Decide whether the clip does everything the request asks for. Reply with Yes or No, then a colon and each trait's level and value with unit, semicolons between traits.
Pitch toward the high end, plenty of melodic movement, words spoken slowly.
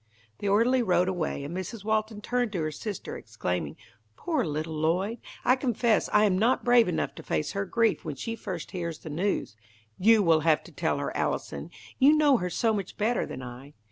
No: high, 195 Hz; wide, 6.2 semitones; fast, 205 wpm